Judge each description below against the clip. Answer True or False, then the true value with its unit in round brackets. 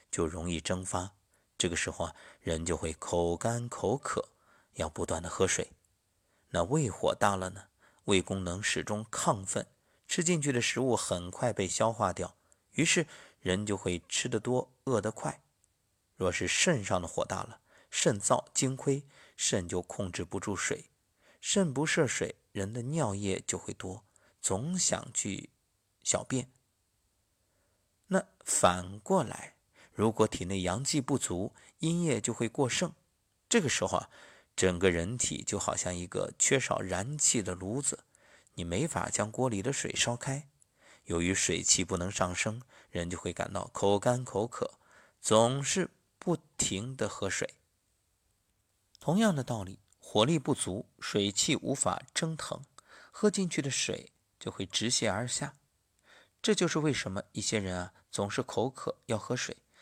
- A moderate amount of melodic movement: False (5.7 semitones)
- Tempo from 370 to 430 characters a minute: False (210 characters per minute)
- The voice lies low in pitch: True (105 Hz)